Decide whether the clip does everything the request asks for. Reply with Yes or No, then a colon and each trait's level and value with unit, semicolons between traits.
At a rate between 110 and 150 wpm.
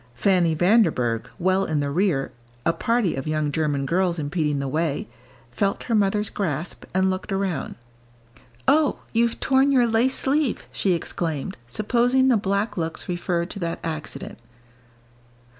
Yes: average, 145 wpm